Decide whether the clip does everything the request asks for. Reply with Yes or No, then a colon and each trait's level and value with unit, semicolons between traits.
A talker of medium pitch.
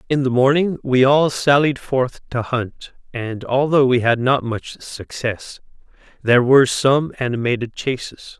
No: low, 130 Hz